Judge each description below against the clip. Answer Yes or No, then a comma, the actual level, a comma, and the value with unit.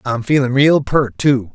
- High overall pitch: No, low, 130 Hz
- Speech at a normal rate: Yes, average, 195 wpm